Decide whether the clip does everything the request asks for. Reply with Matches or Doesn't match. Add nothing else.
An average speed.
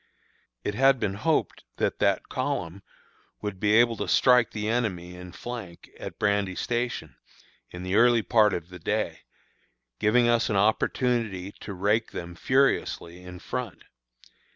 Matches